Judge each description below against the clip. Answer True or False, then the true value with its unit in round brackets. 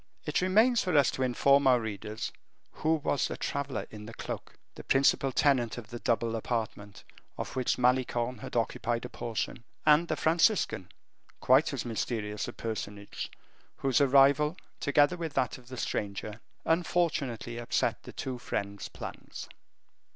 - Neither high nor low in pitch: False (125 Hz)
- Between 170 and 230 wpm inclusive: False (155 wpm)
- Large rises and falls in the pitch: False (3.9 semitones)